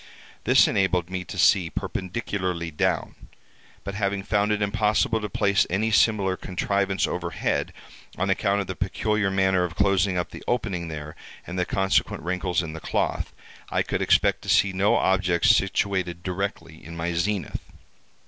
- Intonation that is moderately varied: No, narrow, 2.1 semitones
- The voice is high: No, very low, 95 Hz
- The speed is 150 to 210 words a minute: Yes, average, 160 wpm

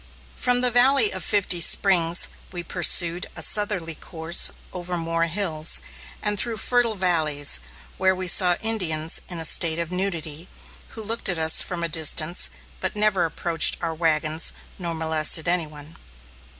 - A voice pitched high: No, medium, 175 Hz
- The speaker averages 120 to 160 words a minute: Yes, average, 155 wpm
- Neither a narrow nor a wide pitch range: Yes, average, 3.3 semitones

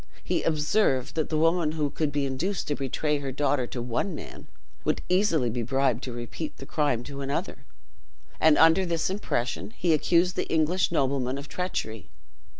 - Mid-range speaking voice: Yes, medium, 150 Hz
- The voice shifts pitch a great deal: No, average, 3.8 semitones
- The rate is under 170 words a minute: No, average, 175 wpm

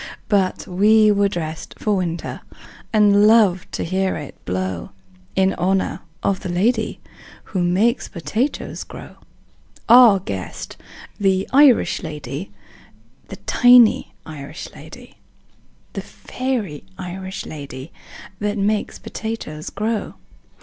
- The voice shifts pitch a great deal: No, average, 4.2 semitones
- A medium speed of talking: No, slow, 110 wpm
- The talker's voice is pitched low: No, high, 195 Hz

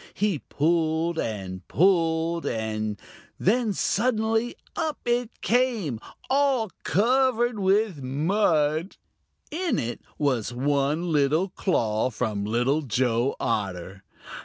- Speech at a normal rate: No, slow, 100 wpm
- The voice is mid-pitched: Yes, medium, 160 Hz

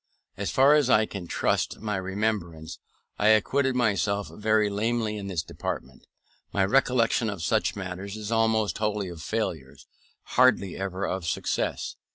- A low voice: Yes, low, 105 Hz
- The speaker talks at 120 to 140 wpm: No, average, 150 wpm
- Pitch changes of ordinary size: Yes, average, 3.0 semitones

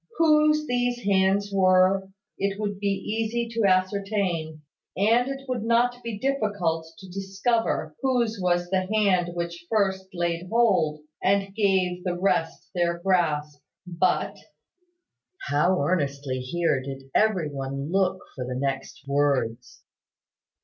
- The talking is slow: Yes, slow, 130 wpm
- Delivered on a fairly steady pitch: No, average, 4.6 semitones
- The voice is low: No, high, 190 Hz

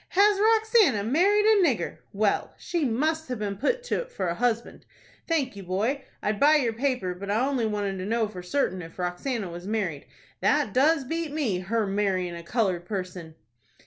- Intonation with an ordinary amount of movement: No, wide, 7.8 semitones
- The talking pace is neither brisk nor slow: Yes, average, 180 wpm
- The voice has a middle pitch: No, high, 225 Hz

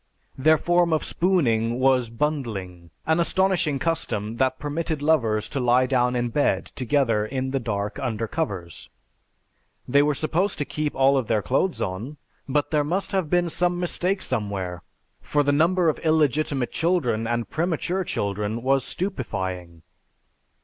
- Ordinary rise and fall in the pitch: No, wide, 6.0 semitones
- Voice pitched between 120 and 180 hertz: Yes, low, 135 Hz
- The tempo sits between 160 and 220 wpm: No, average, 150 wpm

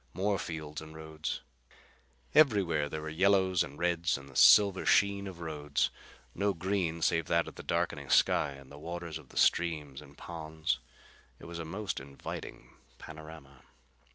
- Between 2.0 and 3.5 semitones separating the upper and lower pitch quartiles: Yes, average, 3.2 semitones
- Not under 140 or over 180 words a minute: Yes, average, 165 wpm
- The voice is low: Yes, very low, 80 Hz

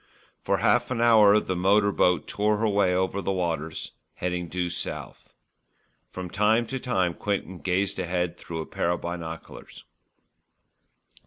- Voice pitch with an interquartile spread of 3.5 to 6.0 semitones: No, average, 2.9 semitones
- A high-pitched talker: No, very low, 95 Hz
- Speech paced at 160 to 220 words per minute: No, average, 150 wpm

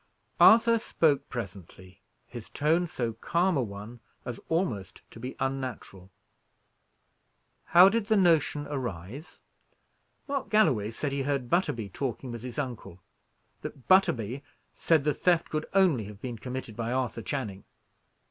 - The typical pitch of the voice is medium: No, low, 130 Hz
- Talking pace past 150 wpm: No, average, 140 wpm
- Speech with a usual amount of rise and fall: No, wide, 6.3 semitones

